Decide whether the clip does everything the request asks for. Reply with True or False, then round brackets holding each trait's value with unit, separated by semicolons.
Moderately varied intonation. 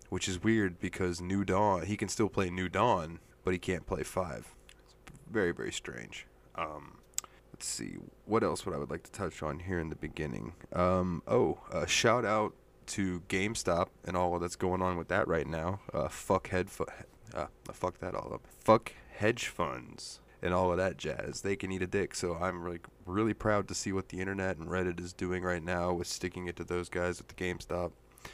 False (1.6 semitones)